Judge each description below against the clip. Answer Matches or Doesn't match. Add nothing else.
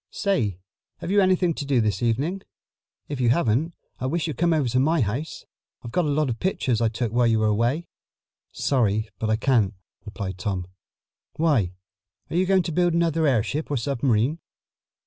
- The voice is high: Doesn't match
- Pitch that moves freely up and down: Matches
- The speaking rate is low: Doesn't match